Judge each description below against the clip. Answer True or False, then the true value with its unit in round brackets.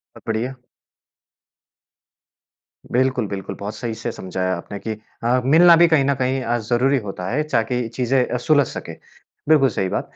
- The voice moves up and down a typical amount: True (3.5 semitones)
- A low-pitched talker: True (125 Hz)